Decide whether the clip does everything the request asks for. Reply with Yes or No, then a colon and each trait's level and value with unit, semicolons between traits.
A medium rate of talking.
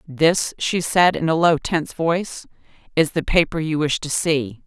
Yes: average, 195 wpm